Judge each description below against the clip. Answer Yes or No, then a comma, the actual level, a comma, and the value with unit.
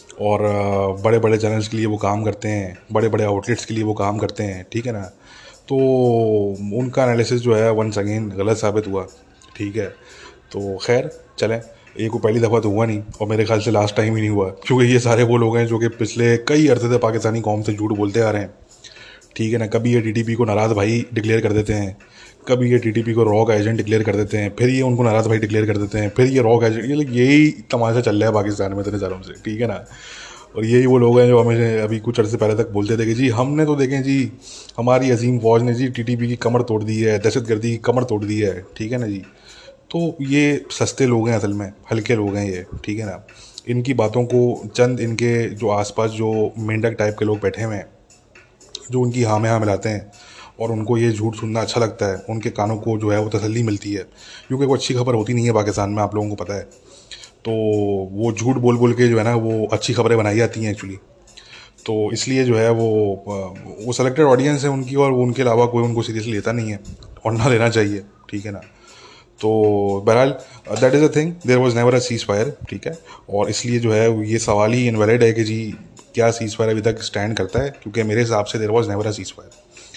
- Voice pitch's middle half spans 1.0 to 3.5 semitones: Yes, narrow, 2.4 semitones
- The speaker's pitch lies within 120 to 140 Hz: No, low, 110 Hz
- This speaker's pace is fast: Yes, fast, 235 wpm